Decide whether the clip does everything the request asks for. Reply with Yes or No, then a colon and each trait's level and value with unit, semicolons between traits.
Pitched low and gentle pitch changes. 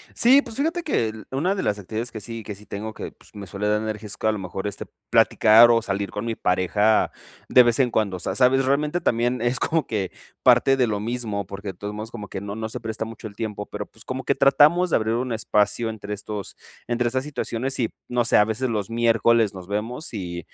No: low, 110 Hz; average, 3.1 semitones